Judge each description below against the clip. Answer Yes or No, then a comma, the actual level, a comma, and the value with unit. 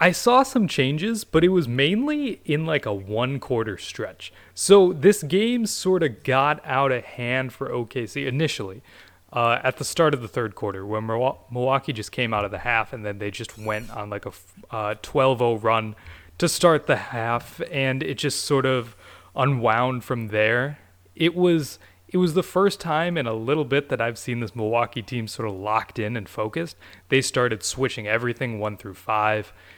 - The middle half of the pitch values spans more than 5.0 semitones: Yes, wide, 5.6 semitones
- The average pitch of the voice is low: Yes, low, 125 Hz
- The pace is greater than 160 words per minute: Yes, average, 190 wpm